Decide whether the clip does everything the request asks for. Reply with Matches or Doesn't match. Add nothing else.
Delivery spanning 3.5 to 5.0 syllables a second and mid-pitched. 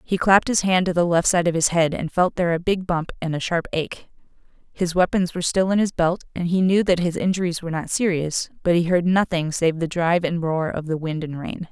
Doesn't match